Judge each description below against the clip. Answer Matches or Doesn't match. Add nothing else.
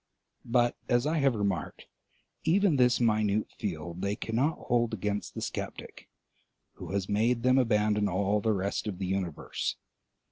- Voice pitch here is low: Matches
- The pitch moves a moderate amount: Matches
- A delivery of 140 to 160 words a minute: Matches